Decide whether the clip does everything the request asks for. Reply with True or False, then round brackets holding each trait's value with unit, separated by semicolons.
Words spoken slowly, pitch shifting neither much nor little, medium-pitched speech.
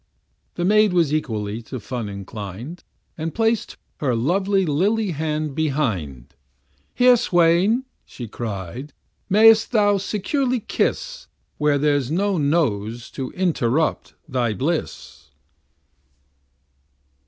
False (105 wpm; 8.6 semitones; 155 Hz)